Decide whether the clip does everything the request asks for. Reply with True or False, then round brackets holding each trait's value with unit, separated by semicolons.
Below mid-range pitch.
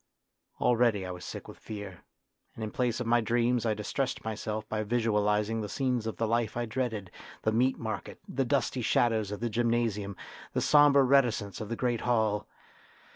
True (115 Hz)